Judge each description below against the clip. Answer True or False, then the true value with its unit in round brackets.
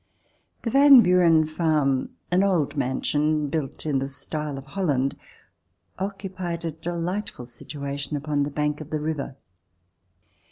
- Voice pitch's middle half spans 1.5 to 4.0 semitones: True (3.6 semitones)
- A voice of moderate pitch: True (155 Hz)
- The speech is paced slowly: True (130 wpm)